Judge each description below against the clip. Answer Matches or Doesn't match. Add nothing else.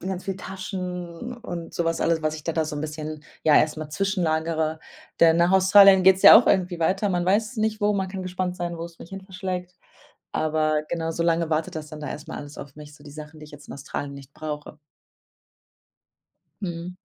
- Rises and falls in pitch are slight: Doesn't match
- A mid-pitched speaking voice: Matches